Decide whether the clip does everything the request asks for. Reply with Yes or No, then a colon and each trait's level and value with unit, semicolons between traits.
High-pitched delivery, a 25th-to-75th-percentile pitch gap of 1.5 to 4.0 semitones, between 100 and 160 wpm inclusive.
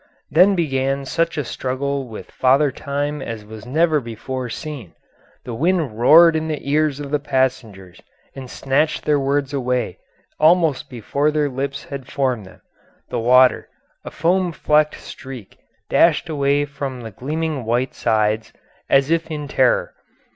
No: medium, 140 Hz; average, 3.2 semitones; average, 150 wpm